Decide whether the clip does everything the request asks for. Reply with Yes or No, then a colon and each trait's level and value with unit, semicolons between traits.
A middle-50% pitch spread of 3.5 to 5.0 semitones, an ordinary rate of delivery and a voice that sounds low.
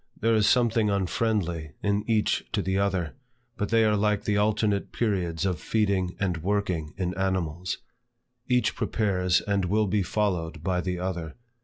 No: average, 2.9 semitones; average, 160 wpm; low, 100 Hz